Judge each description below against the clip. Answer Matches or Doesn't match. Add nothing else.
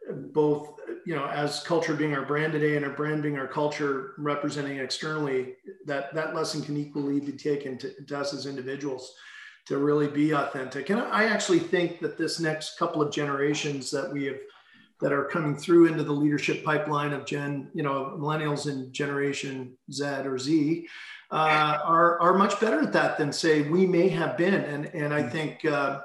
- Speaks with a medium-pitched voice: Matches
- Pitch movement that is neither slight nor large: Doesn't match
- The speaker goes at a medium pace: Matches